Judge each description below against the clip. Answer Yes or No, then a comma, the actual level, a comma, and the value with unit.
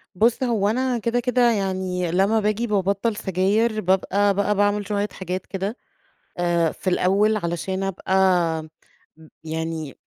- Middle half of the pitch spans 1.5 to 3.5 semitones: Yes, average, 2.7 semitones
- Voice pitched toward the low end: No, high, 200 Hz